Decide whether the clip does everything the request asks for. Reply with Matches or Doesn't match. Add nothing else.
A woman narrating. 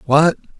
Doesn't match